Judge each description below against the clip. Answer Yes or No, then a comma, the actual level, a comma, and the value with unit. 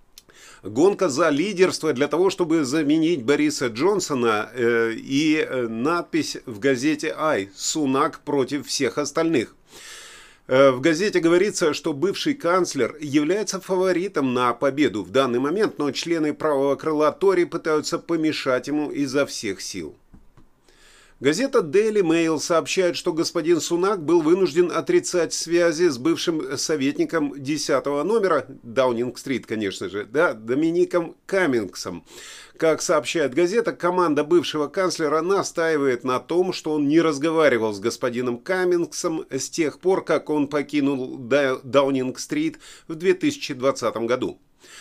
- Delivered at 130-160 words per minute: No, average, 120 wpm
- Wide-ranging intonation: Yes, wide, 6.5 semitones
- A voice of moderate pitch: Yes, medium, 165 Hz